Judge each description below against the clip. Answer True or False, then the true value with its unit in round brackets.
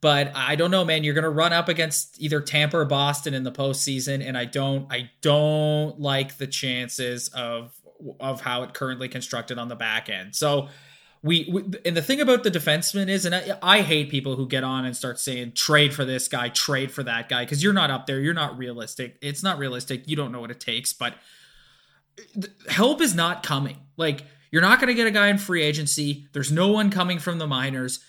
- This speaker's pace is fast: True (220 wpm)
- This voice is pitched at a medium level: True (145 Hz)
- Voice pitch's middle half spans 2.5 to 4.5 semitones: True (4.1 semitones)